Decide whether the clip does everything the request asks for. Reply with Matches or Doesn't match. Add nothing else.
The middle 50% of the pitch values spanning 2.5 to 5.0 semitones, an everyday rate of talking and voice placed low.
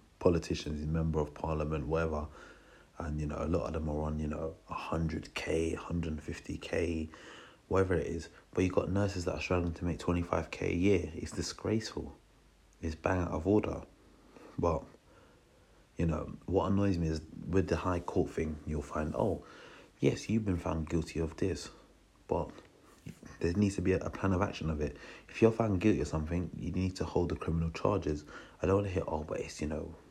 Matches